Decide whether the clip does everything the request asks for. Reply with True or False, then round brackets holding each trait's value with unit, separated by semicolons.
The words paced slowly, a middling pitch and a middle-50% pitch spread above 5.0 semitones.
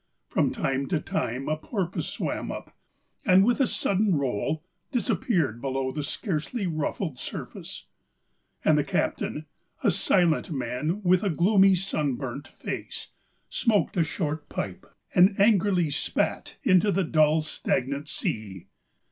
True (130 wpm; 165 Hz; 5.5 semitones)